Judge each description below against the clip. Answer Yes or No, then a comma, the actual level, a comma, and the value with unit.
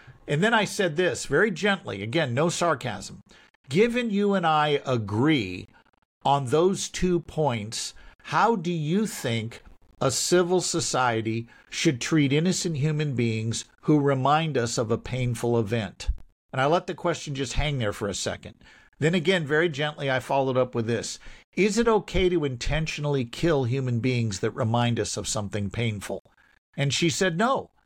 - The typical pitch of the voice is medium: Yes, medium, 145 Hz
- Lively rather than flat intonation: Yes, wide, 6.5 semitones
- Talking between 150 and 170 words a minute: Yes, average, 165 wpm